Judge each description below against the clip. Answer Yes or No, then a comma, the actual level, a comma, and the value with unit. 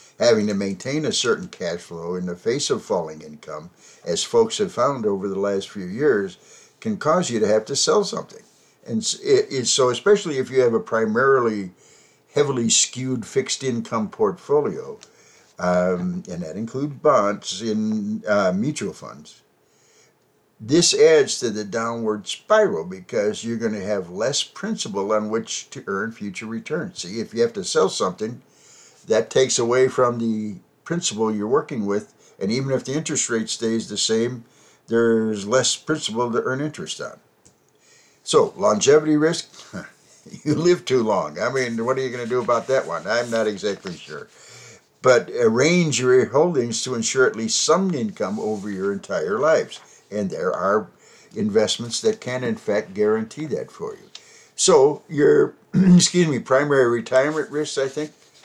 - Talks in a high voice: No, low, 125 Hz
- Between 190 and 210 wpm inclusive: No, average, 165 wpm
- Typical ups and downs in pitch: No, wide, 7.8 semitones